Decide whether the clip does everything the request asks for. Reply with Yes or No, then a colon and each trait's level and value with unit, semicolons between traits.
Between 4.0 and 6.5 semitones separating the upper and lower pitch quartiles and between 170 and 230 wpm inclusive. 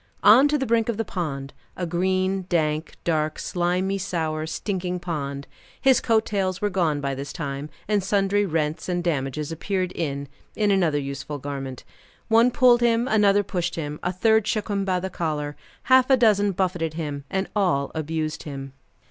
Yes: average, 5.0 semitones; average, 175 wpm